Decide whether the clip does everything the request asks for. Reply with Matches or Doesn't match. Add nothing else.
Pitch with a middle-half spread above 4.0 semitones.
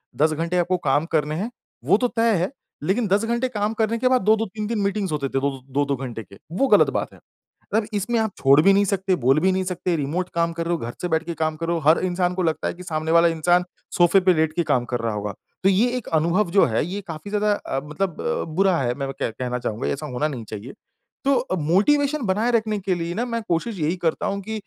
Matches